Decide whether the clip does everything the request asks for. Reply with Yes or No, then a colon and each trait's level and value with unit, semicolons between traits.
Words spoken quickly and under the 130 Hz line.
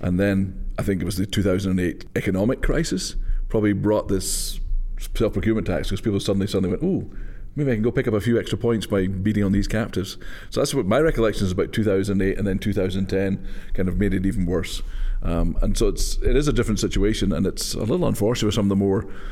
Yes: fast, 225 wpm; low, 100 Hz